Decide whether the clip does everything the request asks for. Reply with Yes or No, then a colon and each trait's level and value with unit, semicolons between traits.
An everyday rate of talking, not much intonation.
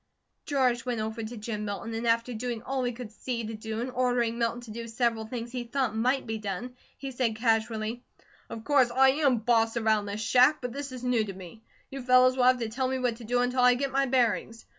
No: fast, 240 wpm; narrow, 2.2 semitones